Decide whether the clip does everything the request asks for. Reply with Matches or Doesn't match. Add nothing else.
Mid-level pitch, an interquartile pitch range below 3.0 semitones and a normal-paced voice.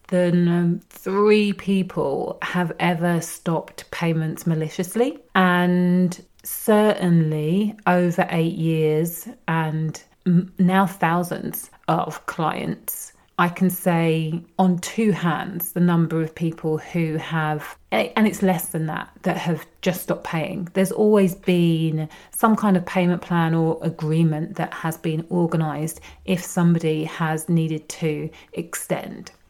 Doesn't match